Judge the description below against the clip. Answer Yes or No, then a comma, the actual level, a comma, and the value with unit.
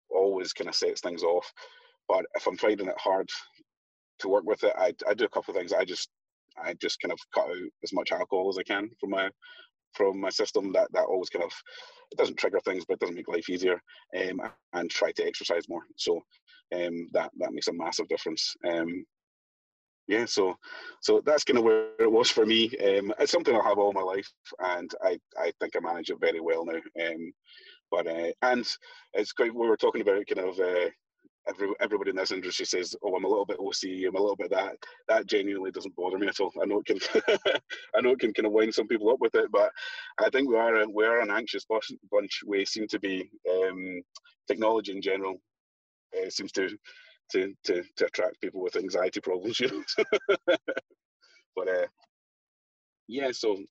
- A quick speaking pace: Yes, fast, 210 wpm